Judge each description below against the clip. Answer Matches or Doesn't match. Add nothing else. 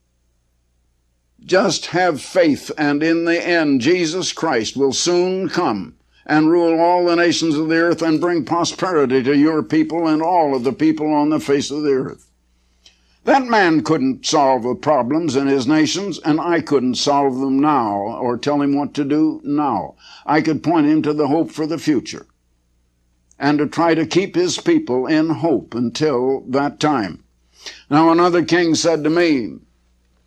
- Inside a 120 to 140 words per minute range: Doesn't match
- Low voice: Doesn't match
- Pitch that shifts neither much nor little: Matches